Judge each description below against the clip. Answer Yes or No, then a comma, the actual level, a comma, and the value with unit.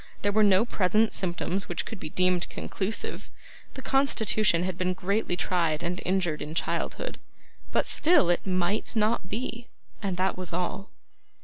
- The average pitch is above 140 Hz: Yes, medium, 185 Hz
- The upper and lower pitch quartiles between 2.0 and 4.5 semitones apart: Yes, average, 3.4 semitones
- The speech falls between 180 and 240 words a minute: No, average, 155 wpm